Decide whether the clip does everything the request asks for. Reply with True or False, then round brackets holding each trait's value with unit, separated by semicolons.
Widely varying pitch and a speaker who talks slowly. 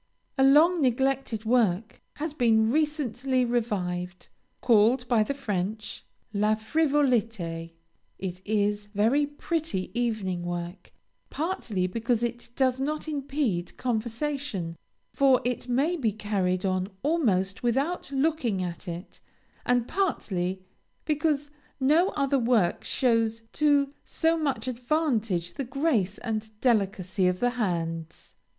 True (6.0 semitones; 120 wpm)